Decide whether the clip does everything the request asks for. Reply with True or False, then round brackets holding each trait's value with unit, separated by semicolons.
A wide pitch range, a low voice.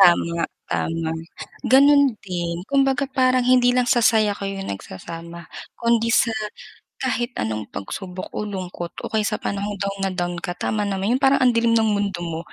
False (5.8 semitones; 205 Hz)